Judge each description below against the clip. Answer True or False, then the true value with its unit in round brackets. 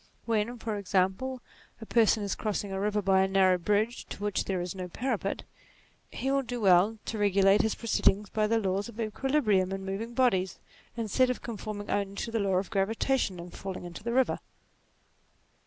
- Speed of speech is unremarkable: True (190 wpm)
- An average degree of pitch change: True (3.1 semitones)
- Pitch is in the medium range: False (205 Hz)